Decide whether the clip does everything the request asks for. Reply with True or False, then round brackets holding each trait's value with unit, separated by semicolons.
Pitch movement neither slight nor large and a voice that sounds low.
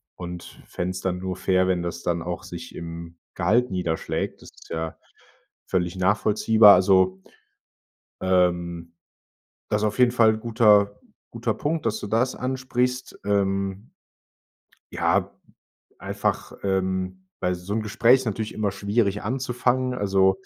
True (3.6 semitones; 100 Hz)